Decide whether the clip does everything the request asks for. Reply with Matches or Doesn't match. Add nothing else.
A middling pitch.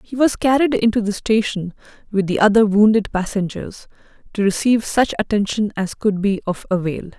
Doesn't match